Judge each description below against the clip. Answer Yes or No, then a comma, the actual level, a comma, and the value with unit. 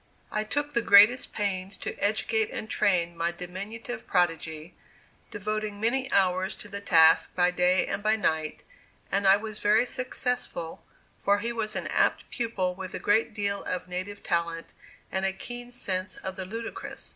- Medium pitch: No, high, 200 Hz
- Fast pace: No, average, 170 wpm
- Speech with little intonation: No, average, 3.3 semitones